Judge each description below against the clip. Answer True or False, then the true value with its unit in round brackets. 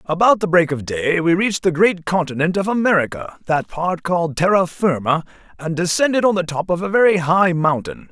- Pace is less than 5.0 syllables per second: False (5.4 syllables/s)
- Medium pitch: True (175 Hz)